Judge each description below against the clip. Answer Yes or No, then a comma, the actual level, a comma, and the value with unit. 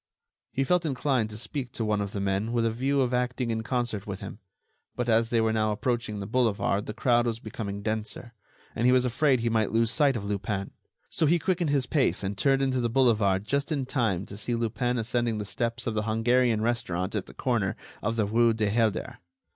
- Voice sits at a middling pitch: No, low, 115 Hz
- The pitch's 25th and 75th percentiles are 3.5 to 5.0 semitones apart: No, average, 2.8 semitones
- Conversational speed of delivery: No, fast, 225 wpm